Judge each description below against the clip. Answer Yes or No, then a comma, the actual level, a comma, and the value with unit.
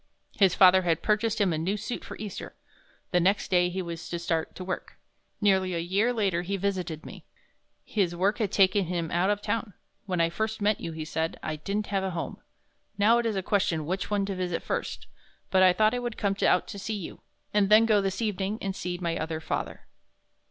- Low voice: No, high, 190 Hz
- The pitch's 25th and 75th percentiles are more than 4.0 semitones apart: No, average, 2.9 semitones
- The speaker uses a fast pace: Yes, fast, 220 wpm